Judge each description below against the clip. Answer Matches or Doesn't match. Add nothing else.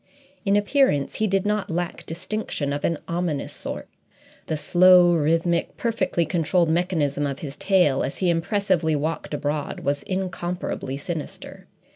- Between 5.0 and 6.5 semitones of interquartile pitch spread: Doesn't match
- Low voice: Doesn't match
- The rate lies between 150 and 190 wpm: Doesn't match